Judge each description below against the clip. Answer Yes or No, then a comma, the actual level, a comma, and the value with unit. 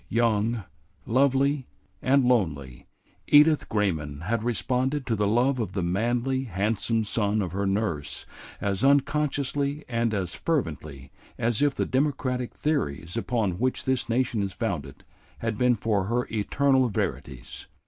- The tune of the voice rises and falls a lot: No, average, 5.0 semitones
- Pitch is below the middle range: Yes, low, 115 Hz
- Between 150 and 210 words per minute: No, average, 140 wpm